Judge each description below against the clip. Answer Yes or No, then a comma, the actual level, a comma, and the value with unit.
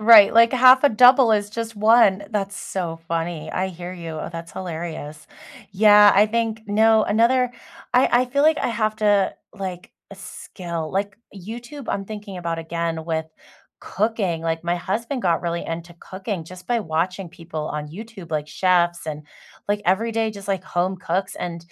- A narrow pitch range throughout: No, average, 4.4 semitones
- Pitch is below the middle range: No, high, 190 Hz